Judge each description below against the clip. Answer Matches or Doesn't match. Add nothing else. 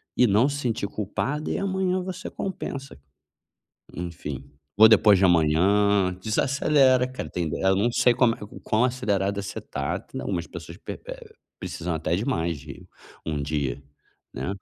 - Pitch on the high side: Doesn't match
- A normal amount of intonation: Doesn't match